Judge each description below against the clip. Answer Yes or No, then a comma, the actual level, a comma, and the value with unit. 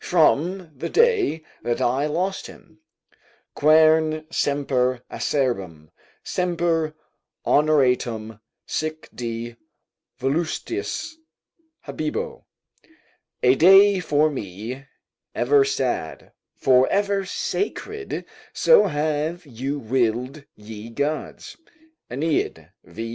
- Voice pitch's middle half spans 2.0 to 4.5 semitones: No, average, 5.3 semitones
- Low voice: No, medium, 150 Hz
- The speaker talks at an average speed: No, slow, 85 wpm